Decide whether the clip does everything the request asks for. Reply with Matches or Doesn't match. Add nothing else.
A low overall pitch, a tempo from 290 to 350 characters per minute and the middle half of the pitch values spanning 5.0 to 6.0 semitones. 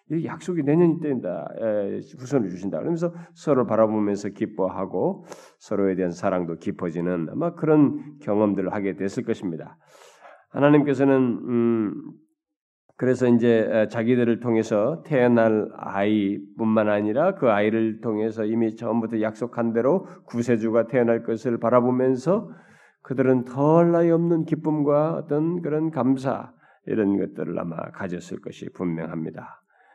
Matches